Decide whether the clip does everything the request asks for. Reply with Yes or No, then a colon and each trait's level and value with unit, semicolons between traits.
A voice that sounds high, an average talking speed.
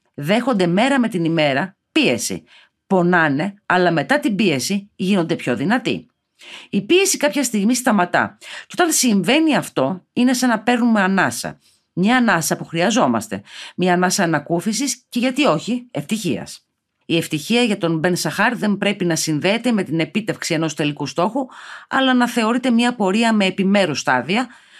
Yes: high, 200 Hz; average, 150 wpm